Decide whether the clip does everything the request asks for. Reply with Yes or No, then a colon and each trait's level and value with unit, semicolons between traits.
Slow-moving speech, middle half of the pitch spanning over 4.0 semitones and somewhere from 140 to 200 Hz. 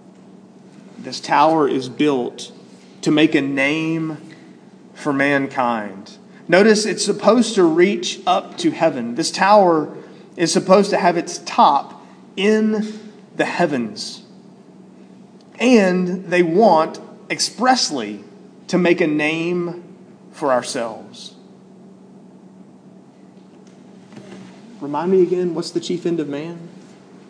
No: slow, 105 wpm; average, 3.7 semitones; medium, 185 Hz